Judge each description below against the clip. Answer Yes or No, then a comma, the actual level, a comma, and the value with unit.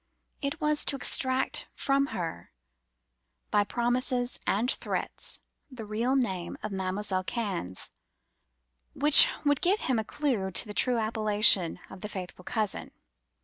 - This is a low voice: No, high, 220 Hz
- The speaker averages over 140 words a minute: No, slow, 135 wpm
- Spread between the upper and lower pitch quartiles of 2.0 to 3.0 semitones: No, average, 5.2 semitones